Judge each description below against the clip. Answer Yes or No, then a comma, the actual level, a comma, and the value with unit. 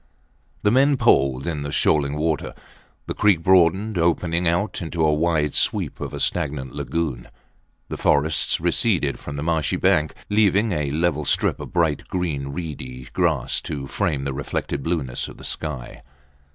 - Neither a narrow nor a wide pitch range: Yes, average, 3.8 semitones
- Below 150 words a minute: No, average, 160 wpm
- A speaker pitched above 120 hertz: No, very low, 80 Hz